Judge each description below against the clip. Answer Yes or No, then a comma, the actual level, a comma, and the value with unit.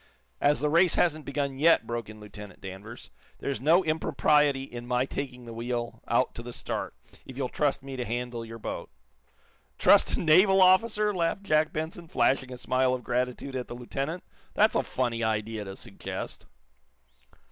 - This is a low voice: Yes, low, 130 Hz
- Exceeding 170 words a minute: Yes, average, 180 wpm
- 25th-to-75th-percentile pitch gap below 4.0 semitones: No, average, 4.5 semitones